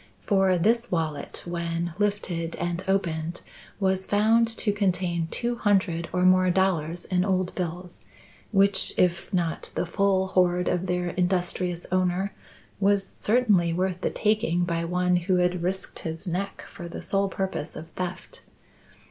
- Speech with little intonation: Yes, narrow, 2.0 semitones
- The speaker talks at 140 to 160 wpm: Yes, average, 150 wpm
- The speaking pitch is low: No, medium, 180 Hz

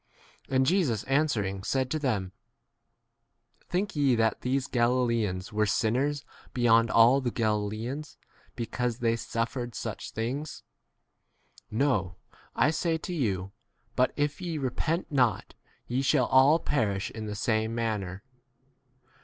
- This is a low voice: Yes, low, 120 Hz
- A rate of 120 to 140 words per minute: Yes, slow, 135 wpm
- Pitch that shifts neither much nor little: Yes, average, 4.2 semitones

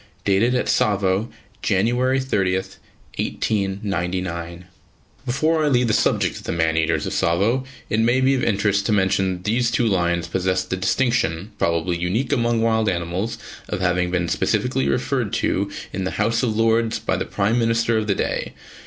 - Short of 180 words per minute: Yes, average, 170 wpm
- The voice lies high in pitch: No, low, 100 Hz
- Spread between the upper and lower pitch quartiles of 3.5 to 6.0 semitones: Yes, average, 4.2 semitones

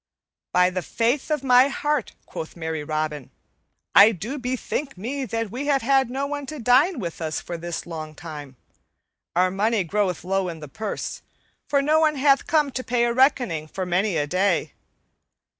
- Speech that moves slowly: No, average, 180 wpm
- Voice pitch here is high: Yes, high, 220 Hz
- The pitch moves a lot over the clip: Yes, wide, 8.0 semitones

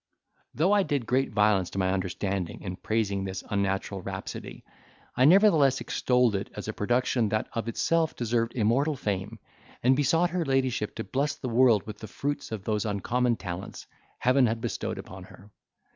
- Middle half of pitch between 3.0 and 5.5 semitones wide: Yes, average, 4.9 semitones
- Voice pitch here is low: Yes, low, 115 Hz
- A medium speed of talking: Yes, average, 175 wpm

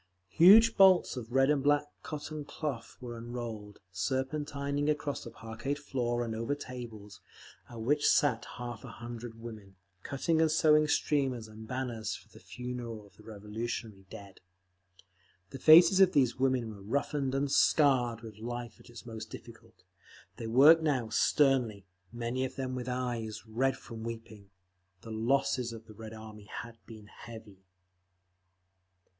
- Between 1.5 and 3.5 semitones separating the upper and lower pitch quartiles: No, average, 3.9 semitones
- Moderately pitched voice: No, low, 120 Hz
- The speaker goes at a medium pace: Yes, average, 150 wpm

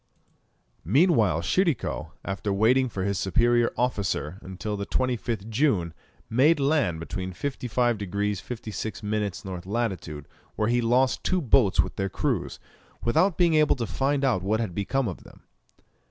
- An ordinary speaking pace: Yes, average, 150 wpm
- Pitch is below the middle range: Yes, low, 110 Hz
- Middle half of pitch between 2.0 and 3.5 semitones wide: No, average, 5.0 semitones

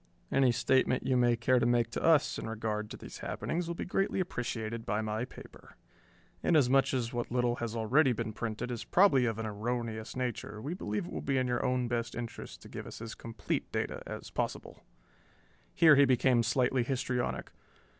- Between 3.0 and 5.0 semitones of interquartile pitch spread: No, narrow, 2.5 semitones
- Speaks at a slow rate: No, average, 195 wpm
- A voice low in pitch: Yes, low, 120 Hz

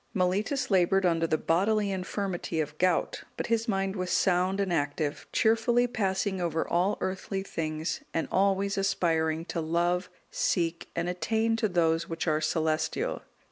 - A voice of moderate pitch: Yes, medium, 180 Hz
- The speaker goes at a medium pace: Yes, average, 150 wpm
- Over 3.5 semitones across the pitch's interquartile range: No, average, 3.2 semitones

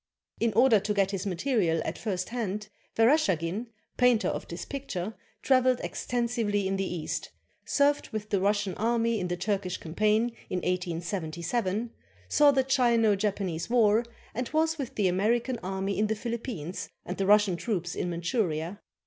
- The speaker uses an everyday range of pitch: Yes, average, 4.4 semitones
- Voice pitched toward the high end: Yes, high, 210 Hz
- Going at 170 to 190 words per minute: No, average, 155 wpm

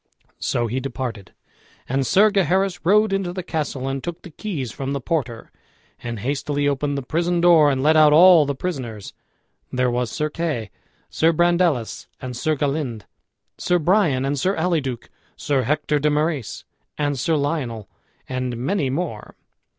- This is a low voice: No, medium, 145 Hz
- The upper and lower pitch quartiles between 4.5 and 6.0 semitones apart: Yes, average, 4.8 semitones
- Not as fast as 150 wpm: No, average, 160 wpm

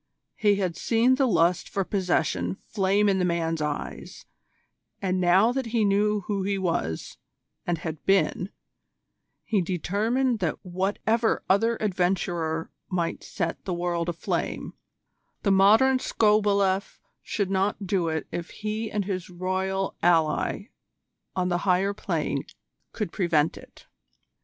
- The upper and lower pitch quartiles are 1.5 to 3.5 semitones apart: Yes, average, 3.0 semitones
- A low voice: No, high, 190 Hz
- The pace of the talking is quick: No, slow, 135 wpm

